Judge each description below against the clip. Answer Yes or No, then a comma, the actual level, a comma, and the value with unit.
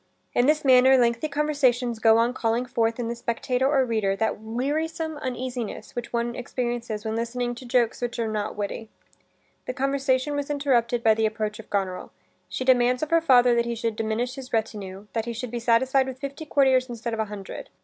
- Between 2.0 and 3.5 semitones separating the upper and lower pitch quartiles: Yes, narrow, 2.6 semitones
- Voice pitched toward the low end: No, high, 240 Hz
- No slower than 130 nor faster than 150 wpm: No, average, 200 wpm